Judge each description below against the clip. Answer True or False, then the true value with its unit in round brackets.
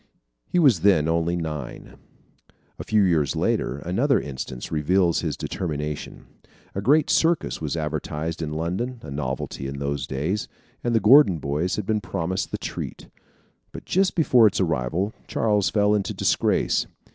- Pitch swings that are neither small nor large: False (5.9 semitones)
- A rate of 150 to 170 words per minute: True (155 wpm)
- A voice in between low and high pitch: False (85 Hz)